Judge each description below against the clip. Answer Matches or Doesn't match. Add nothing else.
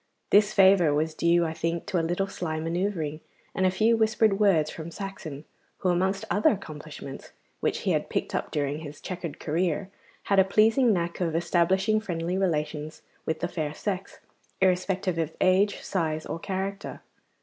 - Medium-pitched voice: Matches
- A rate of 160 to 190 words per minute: Matches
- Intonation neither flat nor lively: Matches